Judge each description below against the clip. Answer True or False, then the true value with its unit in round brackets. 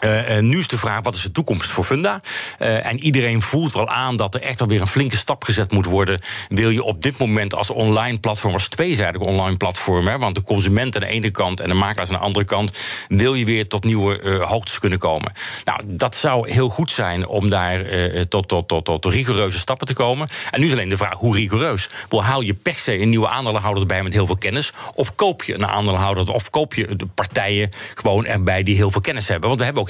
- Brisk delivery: True (245 wpm)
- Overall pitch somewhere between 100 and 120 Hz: True (105 Hz)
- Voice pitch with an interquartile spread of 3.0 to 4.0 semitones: True (3.6 semitones)